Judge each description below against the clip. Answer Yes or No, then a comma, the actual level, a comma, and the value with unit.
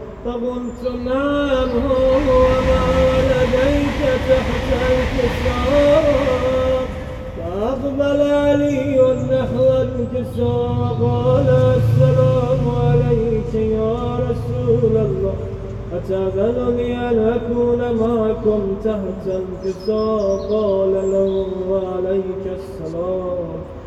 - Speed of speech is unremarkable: No, slow, 70 wpm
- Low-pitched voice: No, high, 195 Hz